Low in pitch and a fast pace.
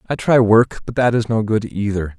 Yes: low, 110 Hz; fast, 250 wpm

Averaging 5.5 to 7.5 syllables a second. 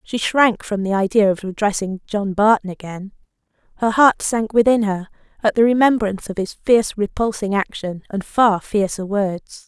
No: 4.9 syllables/s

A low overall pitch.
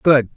Yes: low, 130 Hz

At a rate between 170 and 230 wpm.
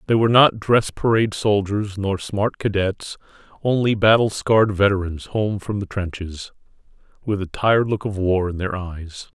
No: average, 160 wpm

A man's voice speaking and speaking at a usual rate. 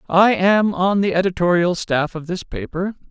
Yes: male; average, 175 wpm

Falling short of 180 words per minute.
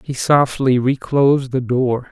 Yes: average, 140 wpm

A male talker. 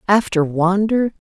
No: female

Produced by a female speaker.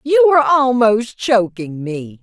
Yes: female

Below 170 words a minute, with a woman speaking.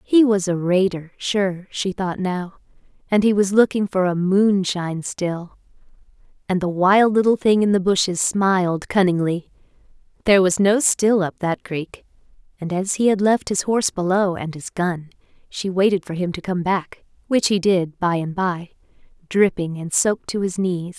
No: average, 175 wpm; female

